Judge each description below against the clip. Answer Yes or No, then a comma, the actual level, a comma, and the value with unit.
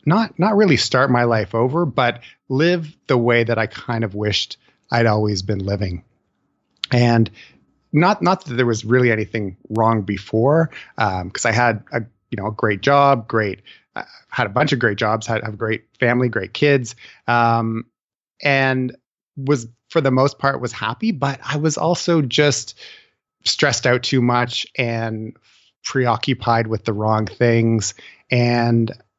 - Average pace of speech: Yes, average, 165 wpm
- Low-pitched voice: Yes, low, 120 Hz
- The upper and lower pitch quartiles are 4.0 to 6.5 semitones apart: No, average, 3.3 semitones